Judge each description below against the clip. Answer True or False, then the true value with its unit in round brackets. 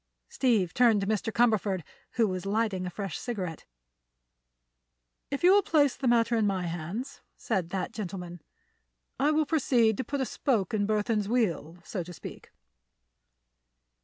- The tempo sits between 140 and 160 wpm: True (155 wpm)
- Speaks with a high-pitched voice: True (215 Hz)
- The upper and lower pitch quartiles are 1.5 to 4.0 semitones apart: False (4.8 semitones)